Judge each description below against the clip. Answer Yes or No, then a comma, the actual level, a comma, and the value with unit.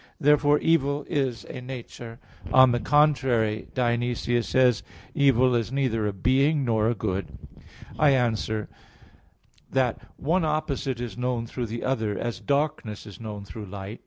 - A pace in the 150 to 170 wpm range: Yes, average, 160 wpm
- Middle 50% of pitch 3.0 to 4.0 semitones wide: Yes, average, 3.7 semitones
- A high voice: No, low, 120 Hz